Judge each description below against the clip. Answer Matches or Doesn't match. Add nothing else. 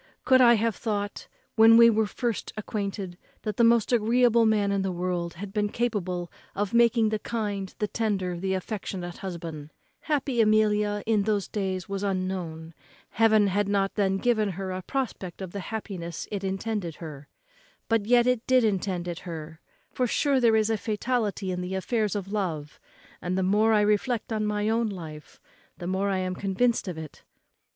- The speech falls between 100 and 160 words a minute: Doesn't match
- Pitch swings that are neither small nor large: Matches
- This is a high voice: Matches